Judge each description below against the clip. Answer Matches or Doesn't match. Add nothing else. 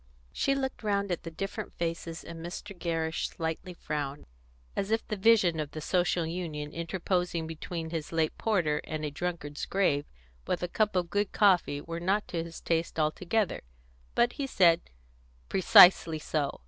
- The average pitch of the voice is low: Doesn't match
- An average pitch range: Matches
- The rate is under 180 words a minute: Matches